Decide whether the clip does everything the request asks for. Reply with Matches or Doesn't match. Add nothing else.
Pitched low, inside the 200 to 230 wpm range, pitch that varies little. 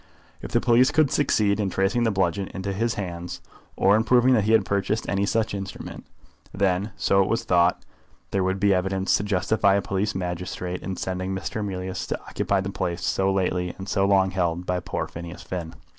Matches